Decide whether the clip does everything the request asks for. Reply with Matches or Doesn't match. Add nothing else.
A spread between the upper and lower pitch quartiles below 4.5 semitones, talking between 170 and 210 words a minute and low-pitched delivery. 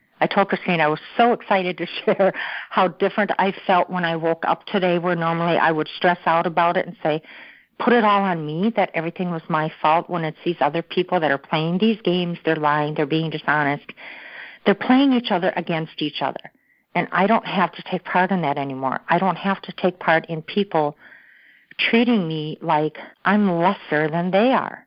Doesn't match